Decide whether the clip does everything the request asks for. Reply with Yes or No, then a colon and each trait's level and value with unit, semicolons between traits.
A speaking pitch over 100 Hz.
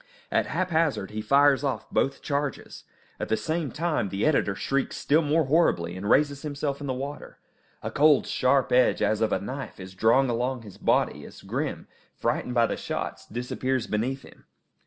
Yes: low, 135 Hz